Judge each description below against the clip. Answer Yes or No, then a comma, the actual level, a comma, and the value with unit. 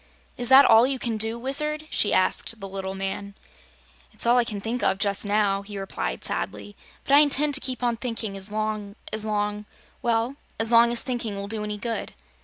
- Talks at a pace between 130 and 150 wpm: No, fast, 205 wpm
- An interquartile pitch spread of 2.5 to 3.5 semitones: Yes, average, 3.2 semitones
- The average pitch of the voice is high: Yes, high, 220 Hz